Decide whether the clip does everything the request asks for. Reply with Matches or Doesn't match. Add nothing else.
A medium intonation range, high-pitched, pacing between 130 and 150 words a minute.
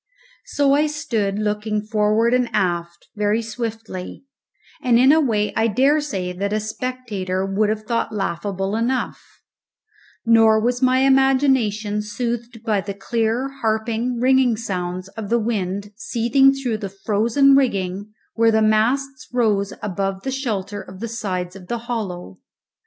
Matches